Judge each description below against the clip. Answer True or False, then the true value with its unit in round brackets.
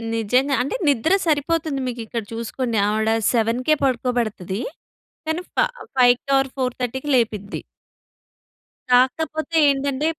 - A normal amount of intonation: True (3.4 semitones)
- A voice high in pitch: True (255 Hz)